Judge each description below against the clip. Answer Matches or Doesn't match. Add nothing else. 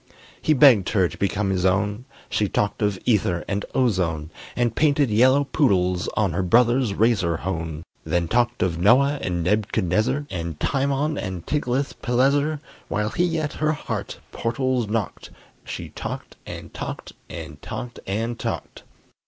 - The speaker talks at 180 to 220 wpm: Doesn't match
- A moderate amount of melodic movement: Doesn't match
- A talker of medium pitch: Doesn't match